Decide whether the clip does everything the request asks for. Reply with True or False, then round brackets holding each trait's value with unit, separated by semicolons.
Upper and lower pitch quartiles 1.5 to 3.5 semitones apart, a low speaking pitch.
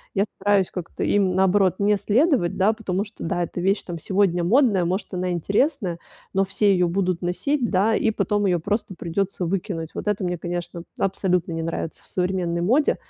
False (2.7 semitones; 190 Hz)